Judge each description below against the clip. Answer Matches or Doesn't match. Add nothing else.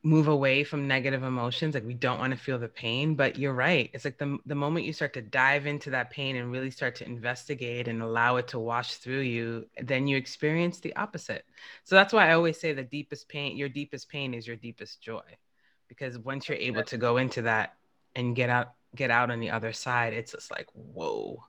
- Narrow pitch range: Doesn't match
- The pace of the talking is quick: Matches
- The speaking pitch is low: Matches